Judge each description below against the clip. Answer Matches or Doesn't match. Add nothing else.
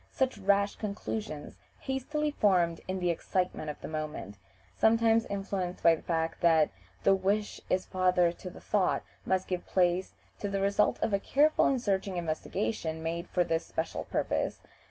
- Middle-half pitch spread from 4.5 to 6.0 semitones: Doesn't match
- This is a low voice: Doesn't match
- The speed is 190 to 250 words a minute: Doesn't match